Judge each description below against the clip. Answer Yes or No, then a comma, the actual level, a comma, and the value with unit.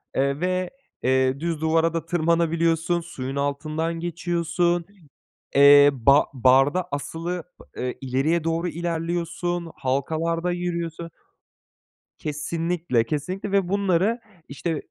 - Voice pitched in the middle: Yes, medium, 165 Hz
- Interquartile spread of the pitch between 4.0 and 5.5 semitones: No, average, 3.3 semitones